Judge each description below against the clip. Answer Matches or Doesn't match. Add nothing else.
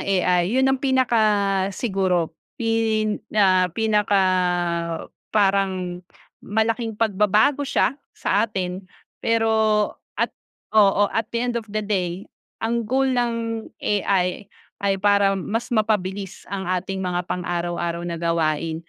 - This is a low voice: Doesn't match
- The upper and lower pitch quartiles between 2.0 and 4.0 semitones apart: Matches